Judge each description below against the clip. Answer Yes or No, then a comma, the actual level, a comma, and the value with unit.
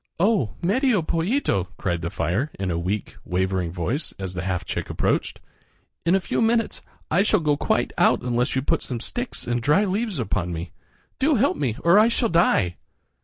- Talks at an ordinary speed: Yes, average, 190 wpm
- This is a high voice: No, low, 135 Hz